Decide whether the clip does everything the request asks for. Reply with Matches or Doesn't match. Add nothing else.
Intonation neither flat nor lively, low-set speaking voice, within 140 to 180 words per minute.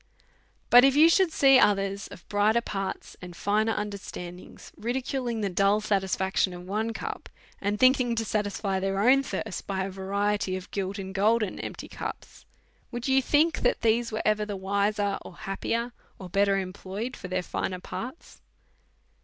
Doesn't match